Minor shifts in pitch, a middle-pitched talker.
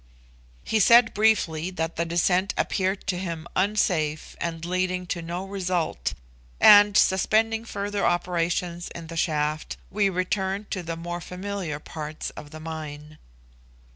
No: average, 3.2 semitones; medium, 180 Hz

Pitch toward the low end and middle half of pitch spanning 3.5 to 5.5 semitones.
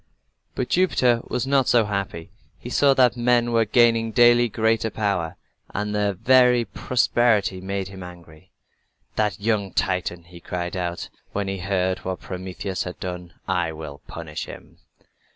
Yes: low, 100 Hz; average, 4.7 semitones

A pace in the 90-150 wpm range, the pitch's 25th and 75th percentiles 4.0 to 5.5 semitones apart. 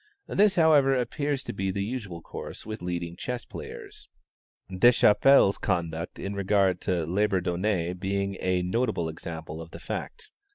Yes: average, 140 wpm; average, 5.2 semitones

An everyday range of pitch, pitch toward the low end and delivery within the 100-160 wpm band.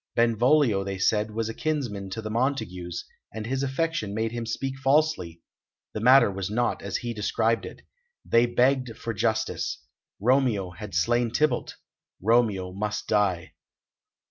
Yes: average, 3.8 semitones; low, 115 Hz; average, 145 wpm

